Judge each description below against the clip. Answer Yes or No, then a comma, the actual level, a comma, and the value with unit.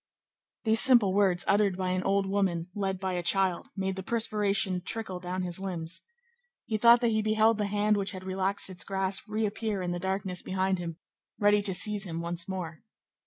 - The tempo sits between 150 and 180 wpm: No, average, 195 wpm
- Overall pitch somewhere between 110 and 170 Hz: No, high, 190 Hz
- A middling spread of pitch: No, narrow, 2.2 semitones